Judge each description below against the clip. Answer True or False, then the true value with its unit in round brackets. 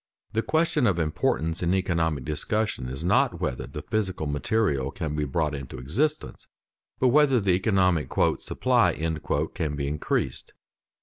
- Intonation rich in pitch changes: True (6.6 semitones)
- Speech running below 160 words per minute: True (140 wpm)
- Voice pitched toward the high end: False (85 Hz)